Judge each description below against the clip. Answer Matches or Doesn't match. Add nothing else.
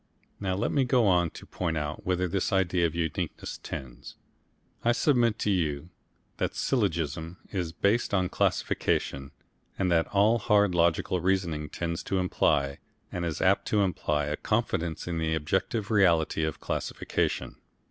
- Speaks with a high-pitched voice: Doesn't match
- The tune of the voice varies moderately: Matches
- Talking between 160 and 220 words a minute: Doesn't match